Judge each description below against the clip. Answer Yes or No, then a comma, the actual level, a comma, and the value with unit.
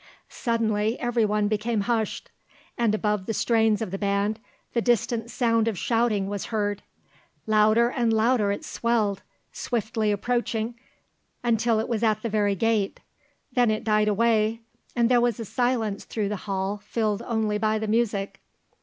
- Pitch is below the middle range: No, high, 220 Hz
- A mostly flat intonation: Yes, narrow, 1.9 semitones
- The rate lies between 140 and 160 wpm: Yes, average, 155 wpm